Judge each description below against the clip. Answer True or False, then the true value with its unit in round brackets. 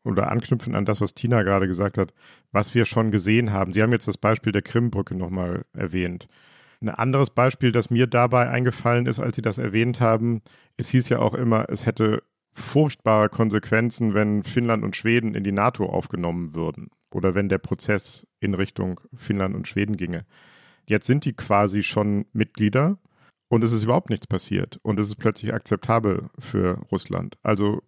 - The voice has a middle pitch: False (110 Hz)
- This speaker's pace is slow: False (180 wpm)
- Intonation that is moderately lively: True (3.0 semitones)